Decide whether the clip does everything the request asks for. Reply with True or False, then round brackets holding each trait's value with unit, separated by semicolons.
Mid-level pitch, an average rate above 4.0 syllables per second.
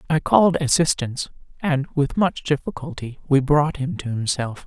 True (150 Hz; 4.9 syllables/s)